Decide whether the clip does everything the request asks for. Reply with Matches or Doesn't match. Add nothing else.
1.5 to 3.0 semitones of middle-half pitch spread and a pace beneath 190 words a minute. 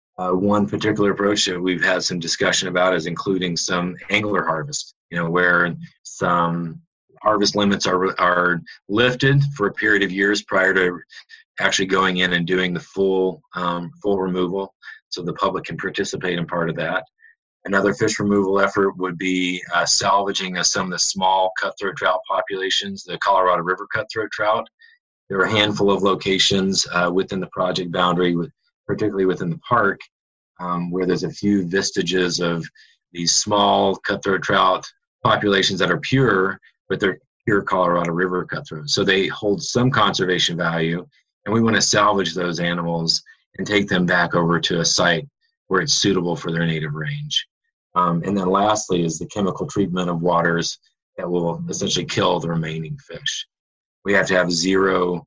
Matches